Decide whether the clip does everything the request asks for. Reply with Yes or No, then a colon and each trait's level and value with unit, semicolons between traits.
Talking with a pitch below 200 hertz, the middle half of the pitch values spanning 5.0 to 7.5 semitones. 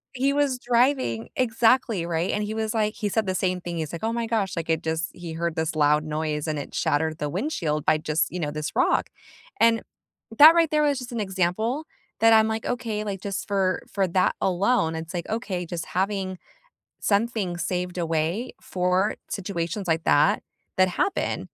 Yes: medium, 185 Hz; wide, 5.4 semitones